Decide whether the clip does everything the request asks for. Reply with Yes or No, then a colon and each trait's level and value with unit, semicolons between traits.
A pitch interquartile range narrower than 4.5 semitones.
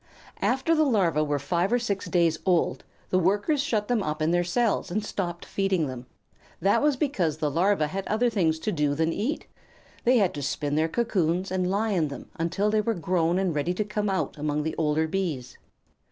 No: average, 4.8 semitones